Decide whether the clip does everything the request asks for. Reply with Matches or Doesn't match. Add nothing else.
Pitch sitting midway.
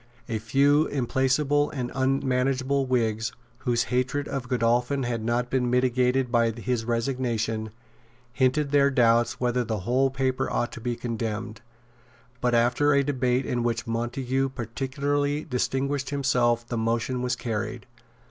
Doesn't match